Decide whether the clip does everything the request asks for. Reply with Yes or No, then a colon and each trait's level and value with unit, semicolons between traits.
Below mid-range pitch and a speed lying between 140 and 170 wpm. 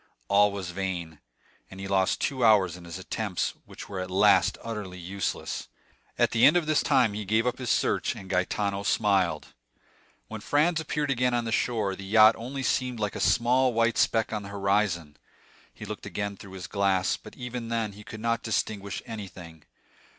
No: low, 105 Hz; average, 190 wpm